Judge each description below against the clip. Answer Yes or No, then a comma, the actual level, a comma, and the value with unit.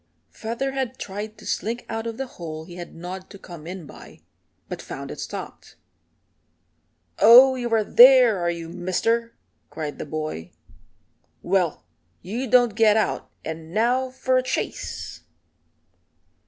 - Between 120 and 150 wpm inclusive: Yes, average, 140 wpm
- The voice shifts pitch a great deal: Yes, wide, 5.8 semitones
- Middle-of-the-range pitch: No, high, 215 Hz